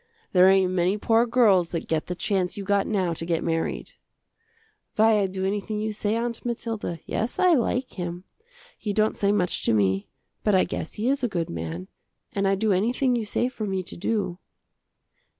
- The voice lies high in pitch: Yes, high, 200 Hz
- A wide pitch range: No, average, 3.9 semitones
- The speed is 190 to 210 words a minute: Yes, average, 200 wpm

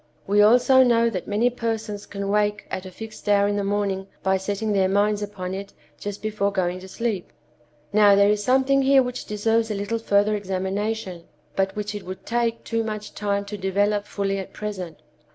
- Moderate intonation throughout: No, narrow, 2.0 semitones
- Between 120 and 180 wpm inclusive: No, average, 195 wpm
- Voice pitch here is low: No, high, 205 Hz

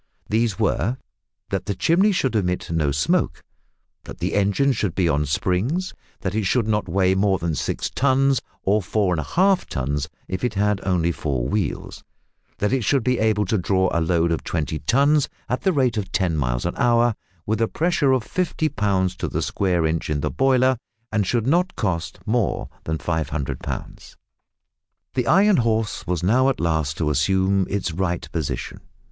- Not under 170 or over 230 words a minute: Yes, average, 190 wpm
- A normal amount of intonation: No, wide, 6.5 semitones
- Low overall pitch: Yes, low, 100 Hz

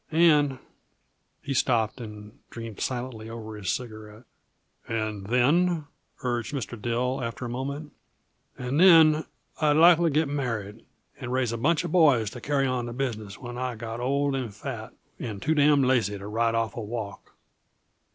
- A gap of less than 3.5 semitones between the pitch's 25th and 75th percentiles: No, average, 4.1 semitones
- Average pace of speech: Yes, average, 165 wpm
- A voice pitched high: No, low, 125 Hz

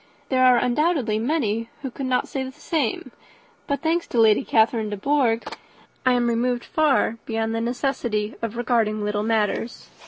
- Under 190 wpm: Yes, average, 165 wpm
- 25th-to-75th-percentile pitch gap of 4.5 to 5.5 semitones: No, average, 2.9 semitones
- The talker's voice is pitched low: No, high, 240 Hz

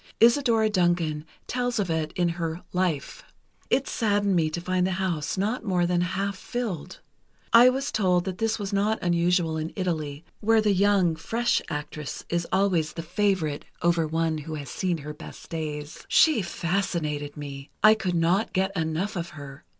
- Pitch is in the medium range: Yes, medium, 175 Hz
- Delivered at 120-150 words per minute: No, average, 175 wpm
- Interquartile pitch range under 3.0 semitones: No, average, 4.0 semitones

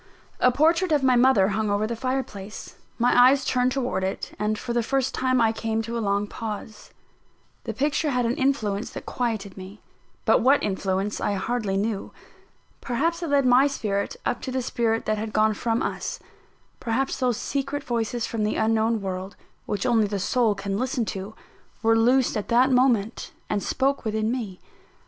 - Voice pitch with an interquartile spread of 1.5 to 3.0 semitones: No, average, 3.5 semitones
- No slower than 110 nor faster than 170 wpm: No, average, 185 wpm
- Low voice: No, high, 230 Hz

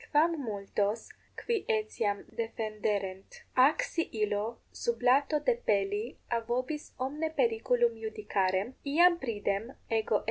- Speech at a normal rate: No, slow, 110 wpm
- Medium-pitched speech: No, high, 235 Hz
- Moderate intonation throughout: No, wide, 7.3 semitones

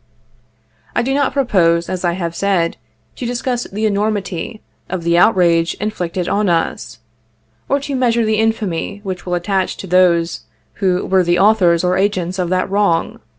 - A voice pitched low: No, high, 190 Hz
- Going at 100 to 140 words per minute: No, average, 165 wpm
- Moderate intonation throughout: Yes, average, 3.8 semitones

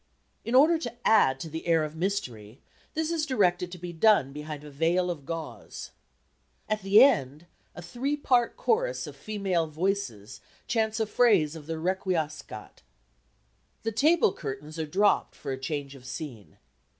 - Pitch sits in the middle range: Yes, medium, 175 Hz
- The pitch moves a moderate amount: No, wide, 6.7 semitones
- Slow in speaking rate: No, average, 160 wpm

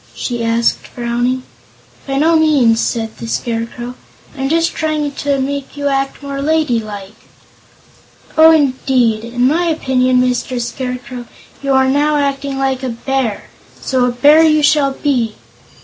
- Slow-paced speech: No, average, 145 wpm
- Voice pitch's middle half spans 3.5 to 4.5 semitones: No, average, 3.0 semitones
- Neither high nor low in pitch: No, very high, 265 Hz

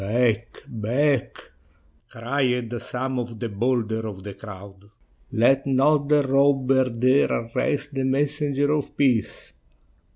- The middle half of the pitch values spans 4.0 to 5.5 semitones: No, average, 3.4 semitones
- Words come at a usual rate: No, slow, 120 wpm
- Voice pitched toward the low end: Yes, low, 130 Hz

